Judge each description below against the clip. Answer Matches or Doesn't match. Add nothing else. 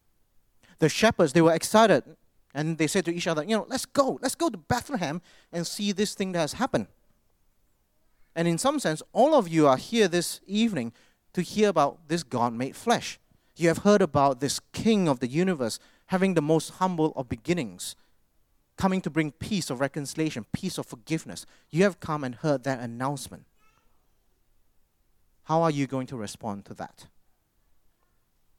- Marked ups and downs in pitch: Matches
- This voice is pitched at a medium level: Matches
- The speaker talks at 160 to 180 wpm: Matches